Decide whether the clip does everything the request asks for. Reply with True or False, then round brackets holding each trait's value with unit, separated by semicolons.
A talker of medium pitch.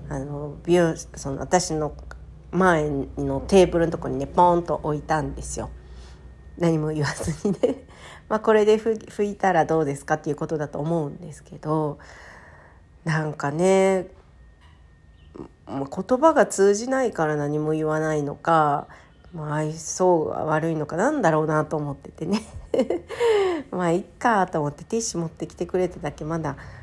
True (155 Hz)